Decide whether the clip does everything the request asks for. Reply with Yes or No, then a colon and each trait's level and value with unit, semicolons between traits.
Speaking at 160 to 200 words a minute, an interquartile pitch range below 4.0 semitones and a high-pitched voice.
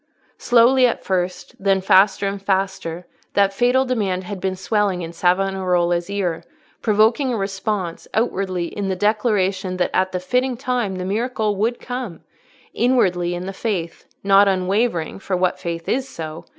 No: average, 150 wpm; average, 3.2 semitones; high, 195 Hz